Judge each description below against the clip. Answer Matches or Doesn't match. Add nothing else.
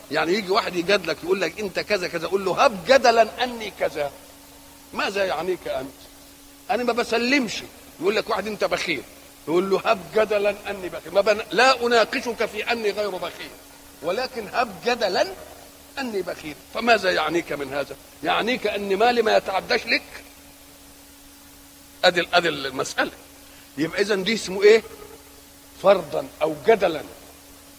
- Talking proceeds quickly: Matches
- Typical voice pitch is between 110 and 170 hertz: Doesn't match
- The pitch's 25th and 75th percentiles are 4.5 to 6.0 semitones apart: Matches